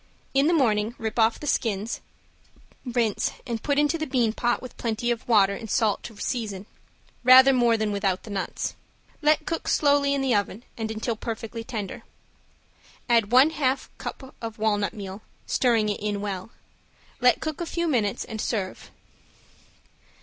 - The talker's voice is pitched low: No, high, 230 Hz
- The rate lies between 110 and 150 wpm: No, average, 165 wpm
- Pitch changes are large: No, average, 3.7 semitones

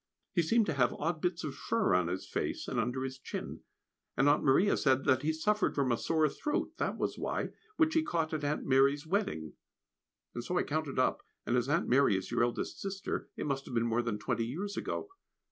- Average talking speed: No, fast, 225 wpm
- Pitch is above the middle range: No, medium, 140 Hz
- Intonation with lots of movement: Yes, wide, 5.8 semitones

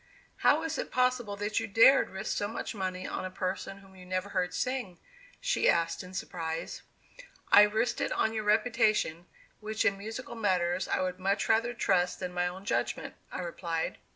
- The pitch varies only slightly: No, average, 3.4 semitones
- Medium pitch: No, high, 195 Hz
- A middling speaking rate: Yes, average, 185 wpm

